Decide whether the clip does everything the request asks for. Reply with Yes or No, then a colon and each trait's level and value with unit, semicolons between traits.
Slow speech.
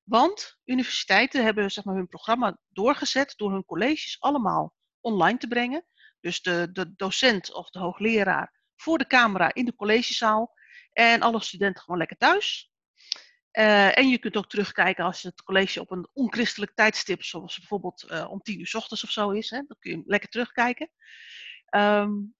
No: average, 170 wpm